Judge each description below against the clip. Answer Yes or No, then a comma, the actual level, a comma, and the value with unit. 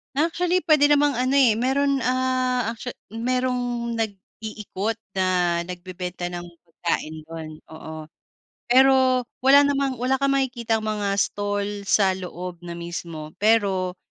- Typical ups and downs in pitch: No, wide, 6.0 semitones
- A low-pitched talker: No, high, 220 Hz